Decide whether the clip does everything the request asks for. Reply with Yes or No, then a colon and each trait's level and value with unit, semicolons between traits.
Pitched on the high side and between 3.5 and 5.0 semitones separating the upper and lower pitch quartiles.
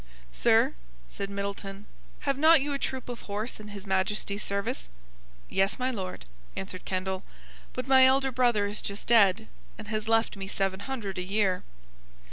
Yes: high, 205 Hz; average, 4.0 semitones